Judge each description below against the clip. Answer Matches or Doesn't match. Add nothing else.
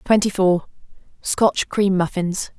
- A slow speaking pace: Matches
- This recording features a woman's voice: Matches